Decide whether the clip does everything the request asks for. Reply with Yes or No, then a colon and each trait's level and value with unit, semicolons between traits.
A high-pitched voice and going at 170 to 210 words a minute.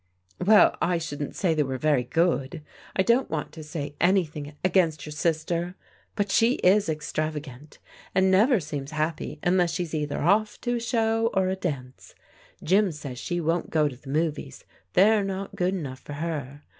No: medium, 165 Hz; average, 180 wpm